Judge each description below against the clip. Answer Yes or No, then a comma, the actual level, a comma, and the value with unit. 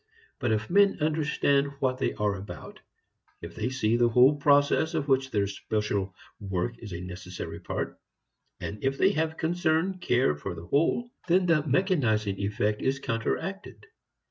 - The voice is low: Yes, low, 130 Hz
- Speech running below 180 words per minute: Yes, average, 160 wpm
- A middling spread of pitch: No, wide, 7.0 semitones